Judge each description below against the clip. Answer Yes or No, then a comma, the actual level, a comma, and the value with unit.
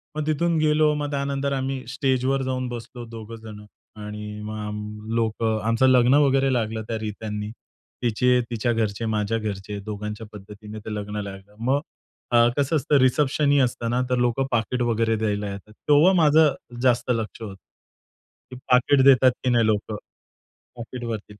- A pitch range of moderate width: Yes, average, 3.9 semitones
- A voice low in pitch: Yes, low, 120 Hz